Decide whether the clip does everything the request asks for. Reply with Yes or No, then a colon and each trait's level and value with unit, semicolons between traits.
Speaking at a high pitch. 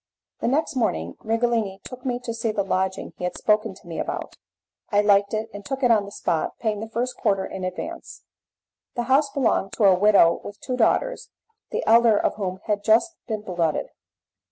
Yes: high, 215 Hz